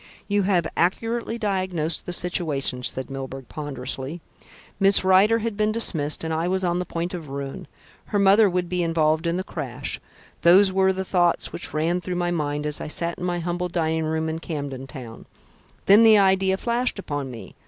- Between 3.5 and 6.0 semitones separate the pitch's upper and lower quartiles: Yes, average, 3.9 semitones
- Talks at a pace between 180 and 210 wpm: Yes, average, 190 wpm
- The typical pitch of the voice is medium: Yes, medium, 175 Hz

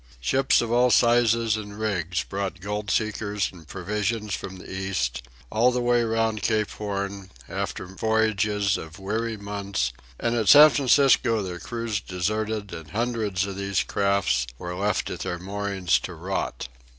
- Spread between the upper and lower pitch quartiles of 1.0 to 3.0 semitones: Yes, average, 2.7 semitones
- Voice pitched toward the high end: No, low, 105 Hz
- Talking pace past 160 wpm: No, average, 155 wpm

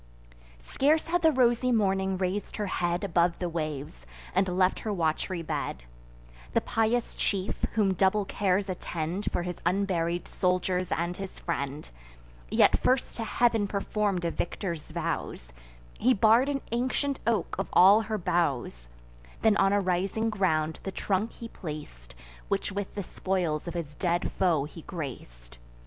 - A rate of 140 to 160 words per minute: Yes, average, 155 wpm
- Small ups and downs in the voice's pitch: No, average, 3.9 semitones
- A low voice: No, medium, 185 Hz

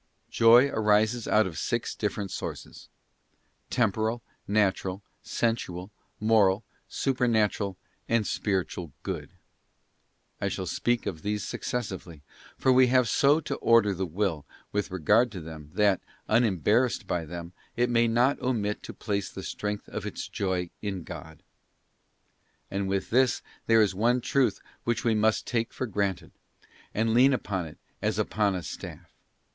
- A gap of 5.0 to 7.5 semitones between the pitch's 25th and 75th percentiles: No, average, 3.7 semitones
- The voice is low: Yes, low, 105 Hz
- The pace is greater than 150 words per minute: No, average, 145 wpm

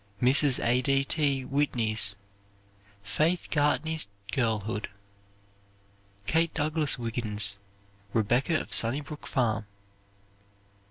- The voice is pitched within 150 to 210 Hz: No, low, 130 Hz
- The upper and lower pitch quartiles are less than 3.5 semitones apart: No, average, 5.0 semitones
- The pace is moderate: No, slow, 85 wpm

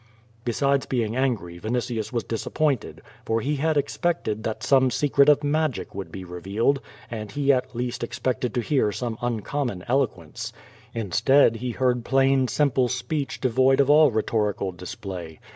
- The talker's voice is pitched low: Yes, low, 125 Hz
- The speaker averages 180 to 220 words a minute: No, average, 155 wpm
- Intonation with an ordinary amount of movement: Yes, average, 4.0 semitones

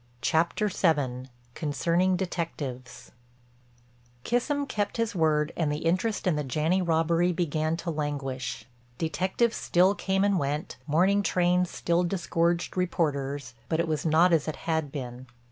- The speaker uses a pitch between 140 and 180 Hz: Yes, medium, 165 Hz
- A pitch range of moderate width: Yes, average, 3.6 semitones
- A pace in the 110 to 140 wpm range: Yes, slow, 135 wpm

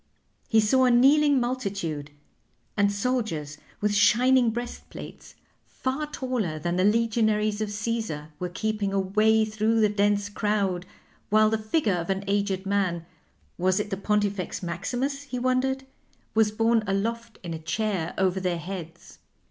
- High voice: Yes, high, 210 Hz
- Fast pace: No, average, 150 wpm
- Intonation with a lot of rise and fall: No, average, 3.4 semitones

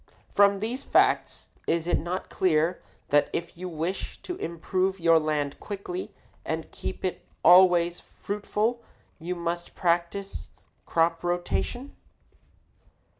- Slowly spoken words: Yes, slow, 120 wpm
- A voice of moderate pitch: Yes, medium, 175 Hz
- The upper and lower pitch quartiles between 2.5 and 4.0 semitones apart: Yes, average, 2.9 semitones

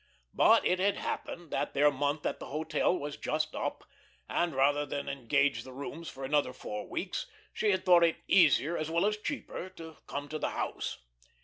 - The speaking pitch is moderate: Yes, medium, 155 Hz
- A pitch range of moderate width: Yes, average, 3.4 semitones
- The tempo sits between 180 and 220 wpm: Yes, average, 195 wpm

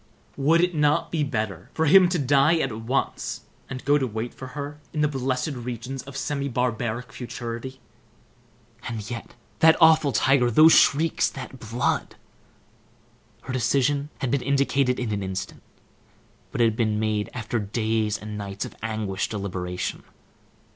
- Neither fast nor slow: Yes, average, 155 wpm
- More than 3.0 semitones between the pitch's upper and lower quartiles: Yes, average, 4.3 semitones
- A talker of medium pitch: No, low, 125 Hz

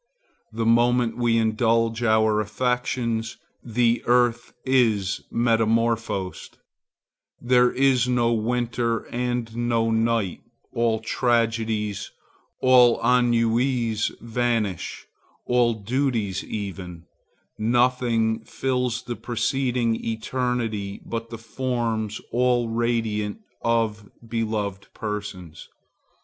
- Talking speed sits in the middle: No, slow, 85 wpm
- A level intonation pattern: Yes, narrow, 1.8 semitones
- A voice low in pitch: Yes, low, 115 Hz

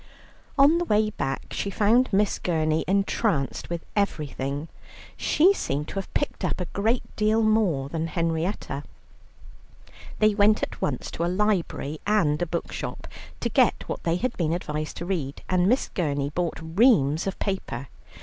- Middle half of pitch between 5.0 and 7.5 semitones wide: Yes, wide, 5.4 semitones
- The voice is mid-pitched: Yes, medium, 175 Hz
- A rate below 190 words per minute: Yes, average, 160 wpm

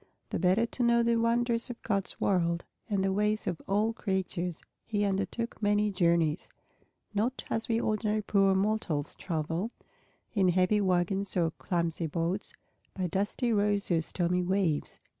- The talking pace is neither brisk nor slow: Yes, average, 150 wpm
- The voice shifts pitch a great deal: No, average, 3.3 semitones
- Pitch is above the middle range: Yes, high, 195 Hz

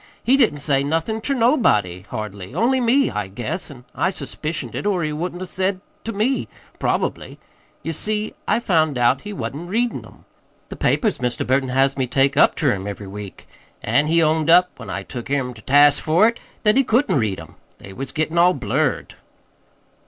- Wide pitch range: Yes, wide, 8.0 semitones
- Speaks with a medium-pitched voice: Yes, medium, 155 Hz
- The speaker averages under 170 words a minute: No, average, 200 wpm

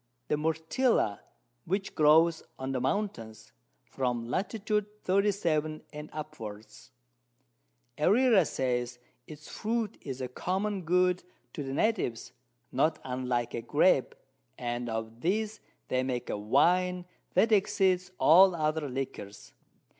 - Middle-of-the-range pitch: Yes, medium, 155 Hz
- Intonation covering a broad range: Yes, wide, 7.5 semitones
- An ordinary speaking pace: No, slow, 115 wpm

